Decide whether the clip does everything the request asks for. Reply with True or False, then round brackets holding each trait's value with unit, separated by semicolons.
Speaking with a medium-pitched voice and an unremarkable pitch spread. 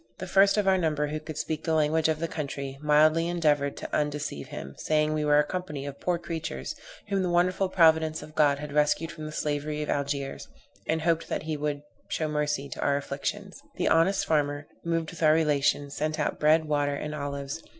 False (150 Hz; 1.9 semitones)